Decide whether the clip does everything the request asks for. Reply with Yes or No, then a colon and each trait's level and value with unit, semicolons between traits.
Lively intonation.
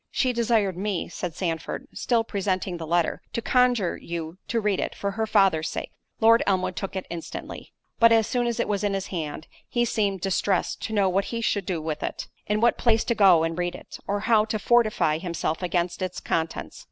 No: average, 4.3 semitones